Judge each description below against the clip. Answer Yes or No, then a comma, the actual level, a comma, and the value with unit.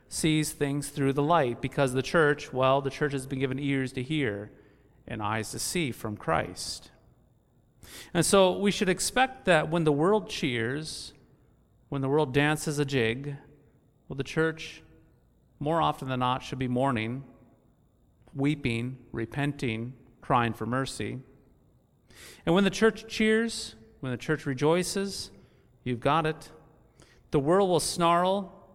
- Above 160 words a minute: No, average, 145 wpm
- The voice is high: No, medium, 140 Hz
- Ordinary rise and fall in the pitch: Yes, average, 4.2 semitones